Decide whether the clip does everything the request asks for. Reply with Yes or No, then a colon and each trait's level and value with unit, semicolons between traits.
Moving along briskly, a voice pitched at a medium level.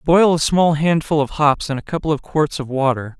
Yes: fast, 245 wpm; medium, 150 Hz